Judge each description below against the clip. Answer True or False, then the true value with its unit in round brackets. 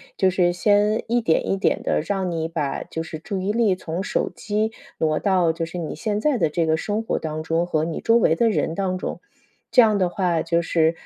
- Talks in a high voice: False (180 Hz)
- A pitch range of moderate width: True (4.2 semitones)